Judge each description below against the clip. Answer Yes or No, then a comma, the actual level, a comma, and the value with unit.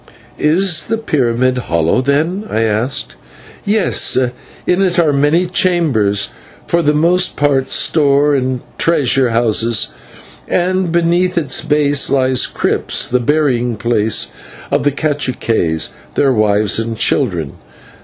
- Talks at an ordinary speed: No, slow, 125 wpm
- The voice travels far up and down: Yes, wide, 6.2 semitones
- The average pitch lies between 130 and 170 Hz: Yes, medium, 140 Hz